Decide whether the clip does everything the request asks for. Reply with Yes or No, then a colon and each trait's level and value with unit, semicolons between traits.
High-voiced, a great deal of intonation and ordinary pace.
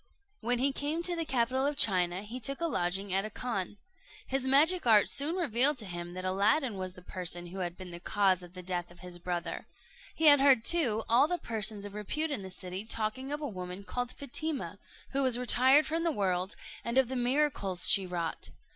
No: high, 220 Hz; wide, 6.9 semitones; fast, 220 wpm